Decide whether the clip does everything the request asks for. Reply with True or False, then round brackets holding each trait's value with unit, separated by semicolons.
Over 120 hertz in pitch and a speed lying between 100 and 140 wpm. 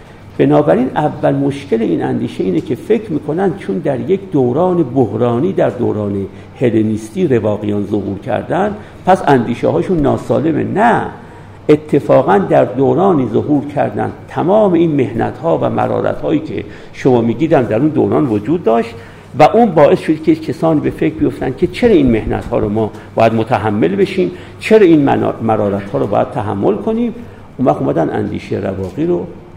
False (135 Hz; 155 wpm)